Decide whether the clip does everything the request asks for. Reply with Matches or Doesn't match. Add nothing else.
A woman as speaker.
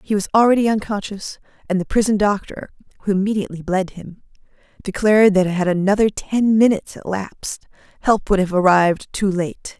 Matches